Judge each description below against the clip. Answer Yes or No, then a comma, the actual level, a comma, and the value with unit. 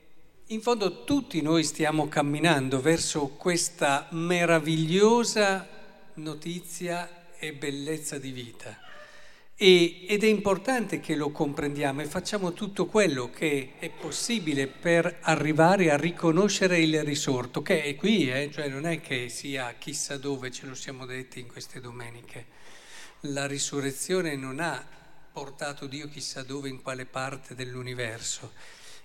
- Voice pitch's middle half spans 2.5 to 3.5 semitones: No, average, 3.9 semitones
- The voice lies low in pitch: No, medium, 155 Hz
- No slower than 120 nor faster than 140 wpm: Yes, average, 130 wpm